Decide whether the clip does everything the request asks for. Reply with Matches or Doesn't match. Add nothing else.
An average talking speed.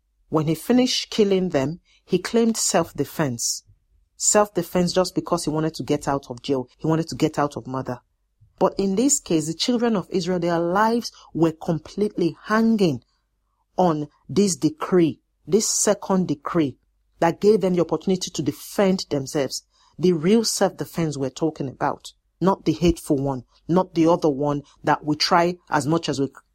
Matches